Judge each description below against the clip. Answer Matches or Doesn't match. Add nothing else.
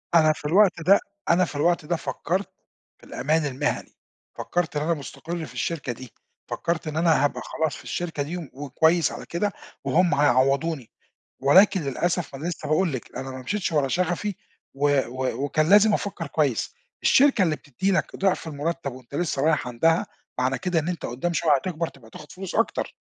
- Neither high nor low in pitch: Matches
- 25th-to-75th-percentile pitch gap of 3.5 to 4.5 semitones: Matches